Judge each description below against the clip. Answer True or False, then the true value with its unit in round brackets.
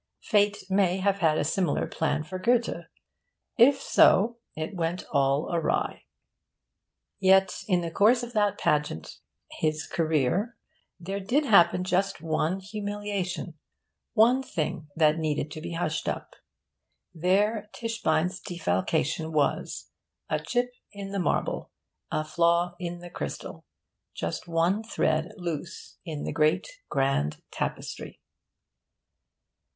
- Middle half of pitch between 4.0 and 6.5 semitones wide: True (4.4 semitones)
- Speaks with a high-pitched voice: False (175 Hz)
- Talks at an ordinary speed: False (125 wpm)